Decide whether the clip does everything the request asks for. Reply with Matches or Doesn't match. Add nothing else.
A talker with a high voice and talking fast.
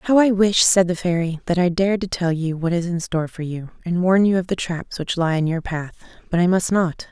Doesn't match